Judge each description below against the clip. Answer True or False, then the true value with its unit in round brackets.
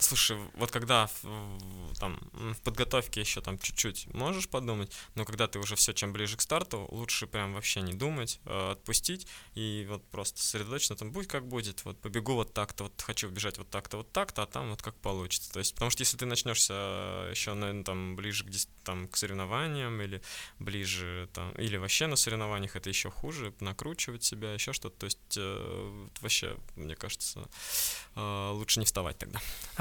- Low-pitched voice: True (105 Hz)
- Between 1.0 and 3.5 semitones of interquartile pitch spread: True (2.9 semitones)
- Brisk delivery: True (180 wpm)